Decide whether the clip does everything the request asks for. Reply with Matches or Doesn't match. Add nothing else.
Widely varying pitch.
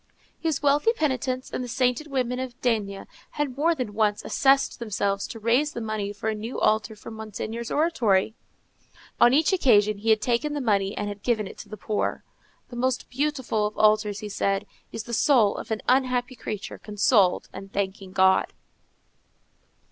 Doesn't match